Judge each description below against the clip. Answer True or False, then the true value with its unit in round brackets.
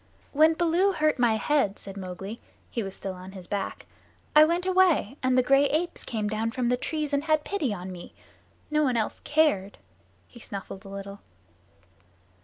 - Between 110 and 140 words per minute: False (185 wpm)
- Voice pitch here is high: True (245 Hz)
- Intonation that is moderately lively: False (7.6 semitones)